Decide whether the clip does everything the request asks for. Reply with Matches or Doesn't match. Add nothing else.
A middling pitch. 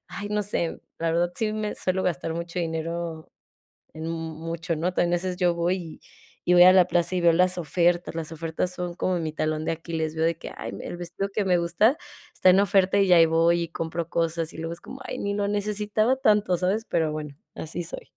Matches